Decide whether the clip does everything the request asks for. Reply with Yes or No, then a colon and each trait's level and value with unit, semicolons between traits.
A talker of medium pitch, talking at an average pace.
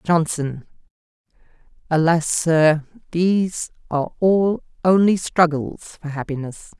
No: medium, 165 Hz; slow, 90 wpm